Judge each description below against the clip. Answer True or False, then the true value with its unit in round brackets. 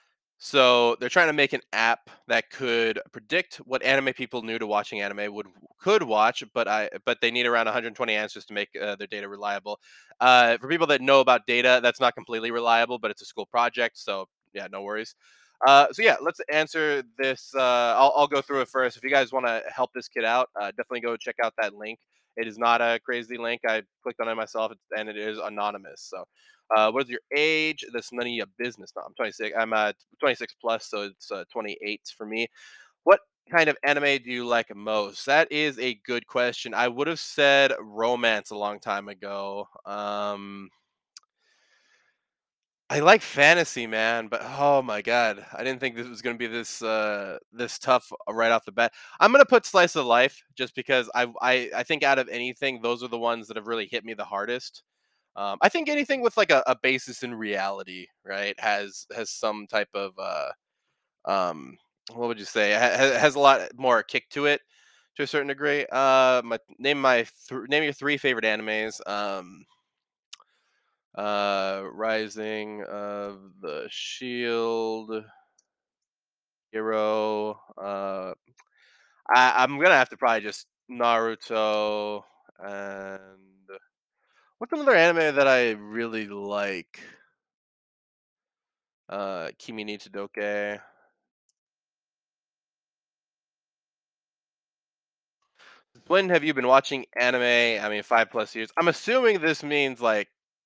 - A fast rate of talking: False (170 wpm)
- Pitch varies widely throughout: False (3.9 semitones)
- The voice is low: True (115 Hz)